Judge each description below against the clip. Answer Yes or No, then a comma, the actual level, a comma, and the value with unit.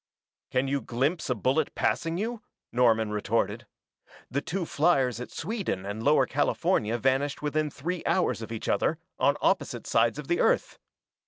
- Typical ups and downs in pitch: No, wide, 5.8 semitones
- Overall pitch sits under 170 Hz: Yes, medium, 140 Hz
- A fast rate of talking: No, average, 160 wpm